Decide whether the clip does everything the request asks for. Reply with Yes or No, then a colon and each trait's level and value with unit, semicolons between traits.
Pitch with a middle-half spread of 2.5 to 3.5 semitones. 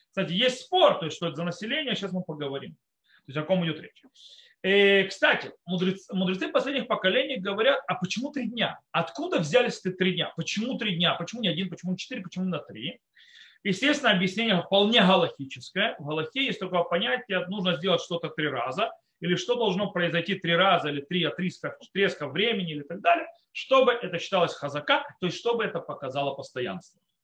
No: average, 4.6 semitones